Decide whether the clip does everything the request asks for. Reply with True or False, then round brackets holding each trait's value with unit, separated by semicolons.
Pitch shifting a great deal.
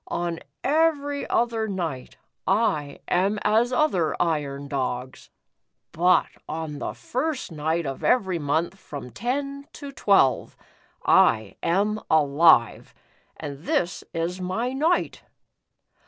True (8.2 semitones)